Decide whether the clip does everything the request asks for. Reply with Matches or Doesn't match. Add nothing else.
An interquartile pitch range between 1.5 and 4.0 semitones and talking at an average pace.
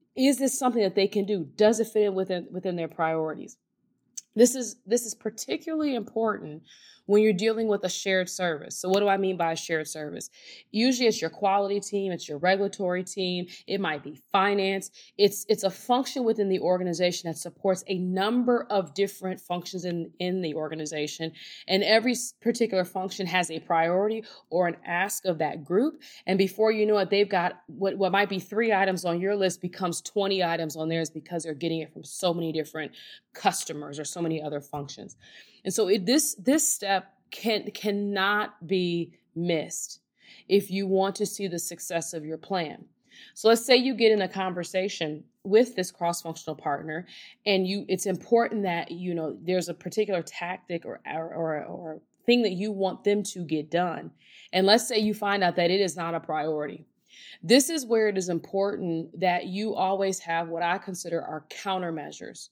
Matches